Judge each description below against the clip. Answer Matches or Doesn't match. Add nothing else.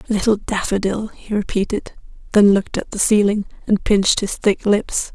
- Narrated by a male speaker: Doesn't match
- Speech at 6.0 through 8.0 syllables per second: Doesn't match